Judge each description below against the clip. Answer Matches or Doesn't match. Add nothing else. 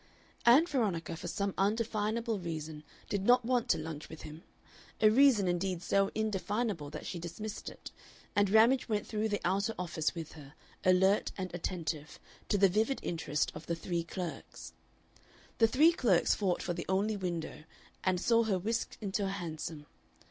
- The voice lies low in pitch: Doesn't match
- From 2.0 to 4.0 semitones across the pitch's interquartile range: Doesn't match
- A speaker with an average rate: Matches